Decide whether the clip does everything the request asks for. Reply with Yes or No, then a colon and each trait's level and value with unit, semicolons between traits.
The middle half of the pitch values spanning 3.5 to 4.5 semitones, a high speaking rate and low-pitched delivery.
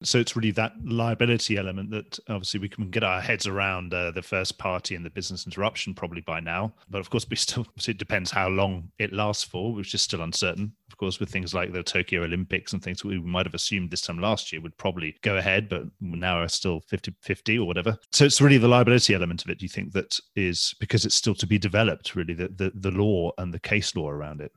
No: average, 3.0 semitones; fast, 250 wpm; low, 100 Hz